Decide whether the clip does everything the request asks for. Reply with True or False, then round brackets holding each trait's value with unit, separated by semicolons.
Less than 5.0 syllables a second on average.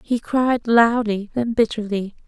True (3.9 syllables/s)